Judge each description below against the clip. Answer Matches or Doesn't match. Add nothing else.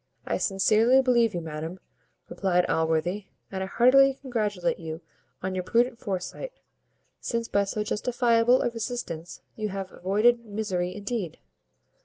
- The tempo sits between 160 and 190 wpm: Doesn't match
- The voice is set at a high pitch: Matches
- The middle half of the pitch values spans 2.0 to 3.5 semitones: Doesn't match